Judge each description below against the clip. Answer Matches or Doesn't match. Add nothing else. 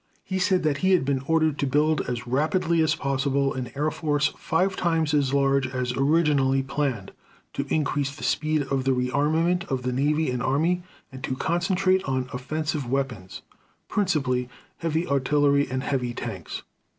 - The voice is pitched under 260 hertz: Matches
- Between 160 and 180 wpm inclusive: Matches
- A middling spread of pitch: Matches